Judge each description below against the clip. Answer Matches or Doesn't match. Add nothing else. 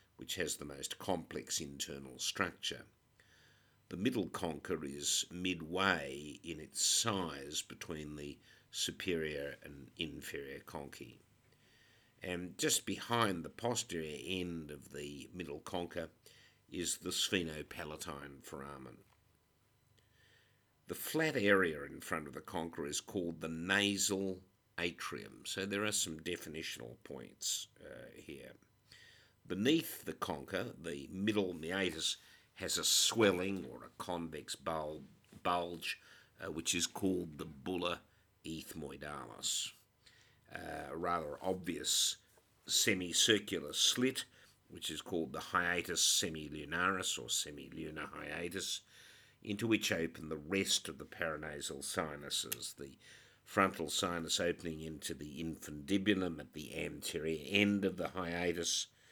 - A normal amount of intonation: Matches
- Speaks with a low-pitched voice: Matches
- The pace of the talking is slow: Matches